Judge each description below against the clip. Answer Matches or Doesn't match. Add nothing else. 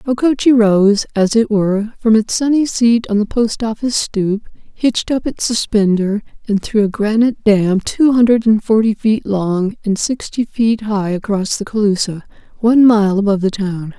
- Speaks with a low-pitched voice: Doesn't match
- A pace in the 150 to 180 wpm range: Matches